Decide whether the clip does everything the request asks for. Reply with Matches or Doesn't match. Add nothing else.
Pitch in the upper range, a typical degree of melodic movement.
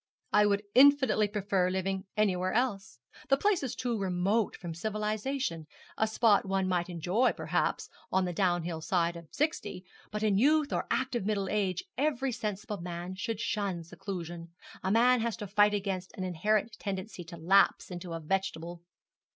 Matches